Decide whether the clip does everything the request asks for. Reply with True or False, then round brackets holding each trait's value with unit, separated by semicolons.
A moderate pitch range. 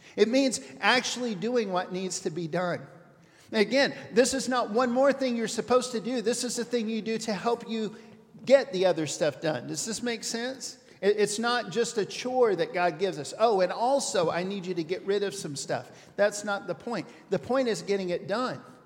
True (4.8 semitones)